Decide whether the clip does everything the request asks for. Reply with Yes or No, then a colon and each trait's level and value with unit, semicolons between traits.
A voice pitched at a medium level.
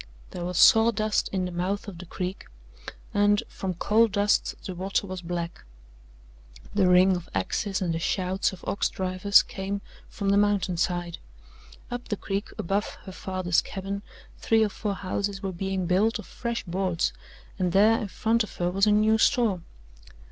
No: high, 195 Hz